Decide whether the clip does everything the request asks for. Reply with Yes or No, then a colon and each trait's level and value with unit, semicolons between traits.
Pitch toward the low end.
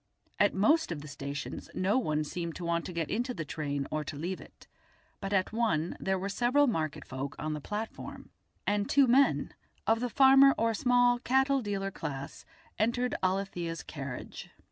No: high, 195 Hz